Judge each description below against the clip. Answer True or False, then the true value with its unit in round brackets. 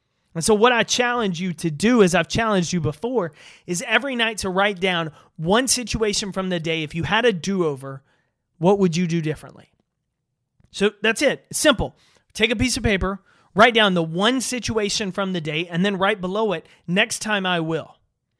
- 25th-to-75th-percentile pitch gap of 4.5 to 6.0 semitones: True (4.9 semitones)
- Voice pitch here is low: False (190 Hz)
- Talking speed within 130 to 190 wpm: False (200 wpm)